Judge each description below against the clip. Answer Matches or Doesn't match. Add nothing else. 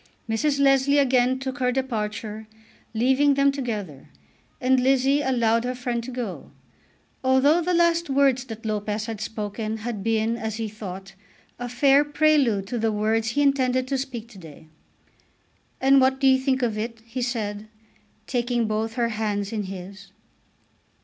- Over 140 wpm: Matches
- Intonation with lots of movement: Doesn't match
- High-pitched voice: Matches